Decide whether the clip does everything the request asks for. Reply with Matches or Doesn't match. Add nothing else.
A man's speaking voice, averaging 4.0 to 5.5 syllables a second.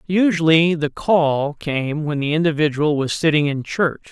Matches